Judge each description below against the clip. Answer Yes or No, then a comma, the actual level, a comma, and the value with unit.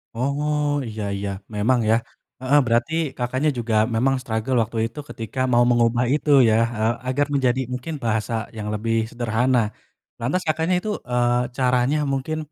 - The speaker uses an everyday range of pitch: Yes, average, 3.0 semitones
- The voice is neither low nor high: No, low, 125 Hz